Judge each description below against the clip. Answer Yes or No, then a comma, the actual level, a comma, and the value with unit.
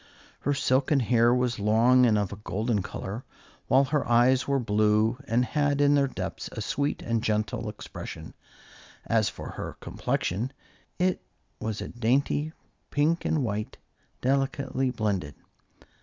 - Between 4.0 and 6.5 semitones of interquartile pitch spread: Yes, average, 4.3 semitones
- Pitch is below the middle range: Yes, low, 125 Hz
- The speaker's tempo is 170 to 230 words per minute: No, average, 140 wpm